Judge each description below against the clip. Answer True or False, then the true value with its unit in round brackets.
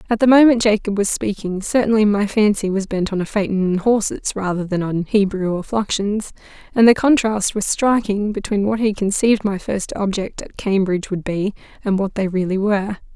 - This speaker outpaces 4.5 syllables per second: True (5.3 syllables/s)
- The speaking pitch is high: True (205 Hz)